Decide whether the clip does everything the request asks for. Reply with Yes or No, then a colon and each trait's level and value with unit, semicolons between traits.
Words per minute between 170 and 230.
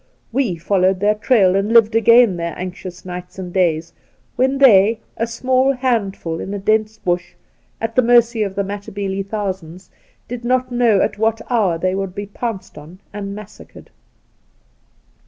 No: average, 160 wpm